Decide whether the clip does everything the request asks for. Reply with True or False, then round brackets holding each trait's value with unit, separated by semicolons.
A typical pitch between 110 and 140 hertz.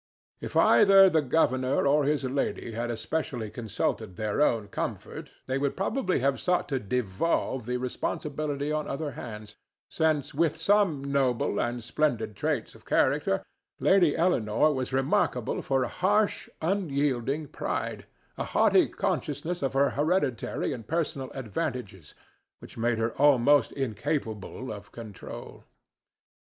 True (135 Hz)